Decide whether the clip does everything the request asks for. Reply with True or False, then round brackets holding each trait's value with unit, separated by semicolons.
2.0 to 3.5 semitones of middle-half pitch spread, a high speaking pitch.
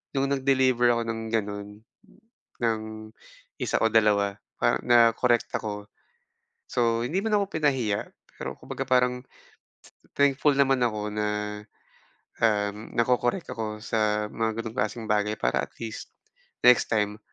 False (2.9 semitones; 115 Hz)